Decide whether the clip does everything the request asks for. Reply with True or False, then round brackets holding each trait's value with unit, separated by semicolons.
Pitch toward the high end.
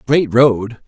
False (120 Hz)